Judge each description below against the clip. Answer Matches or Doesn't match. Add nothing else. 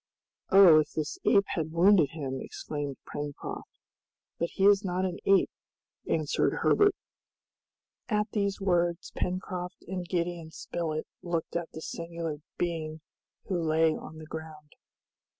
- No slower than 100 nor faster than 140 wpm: Matches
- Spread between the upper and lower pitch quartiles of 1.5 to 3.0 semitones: Matches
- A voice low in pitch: Doesn't match